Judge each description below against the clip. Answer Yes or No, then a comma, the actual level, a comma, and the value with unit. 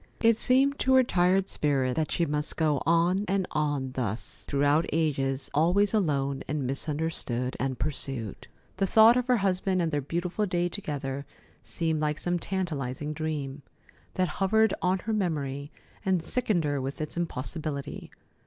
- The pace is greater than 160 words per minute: No, average, 155 wpm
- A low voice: No, medium, 160 Hz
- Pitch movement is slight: No, average, 5.0 semitones